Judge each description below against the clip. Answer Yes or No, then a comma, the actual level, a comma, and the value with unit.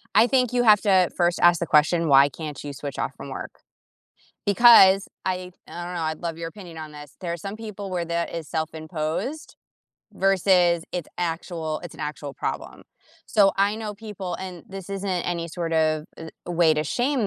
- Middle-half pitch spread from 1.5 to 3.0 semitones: No, average, 3.5 semitones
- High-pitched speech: No, medium, 175 Hz